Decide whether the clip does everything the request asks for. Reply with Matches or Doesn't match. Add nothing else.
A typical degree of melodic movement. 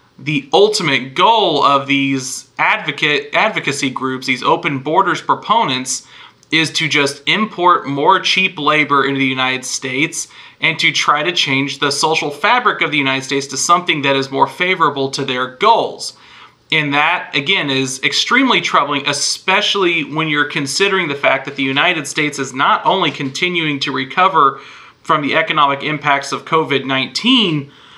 Matches